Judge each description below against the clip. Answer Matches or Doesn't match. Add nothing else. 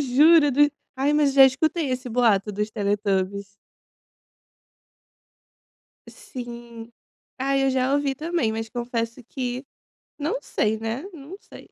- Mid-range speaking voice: Doesn't match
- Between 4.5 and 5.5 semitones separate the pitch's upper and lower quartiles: Doesn't match